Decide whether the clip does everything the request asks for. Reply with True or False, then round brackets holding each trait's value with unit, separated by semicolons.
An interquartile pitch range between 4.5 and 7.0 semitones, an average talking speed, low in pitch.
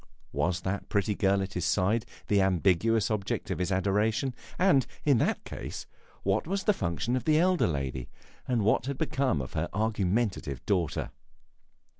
True (4.9 semitones; 165 wpm; 100 Hz)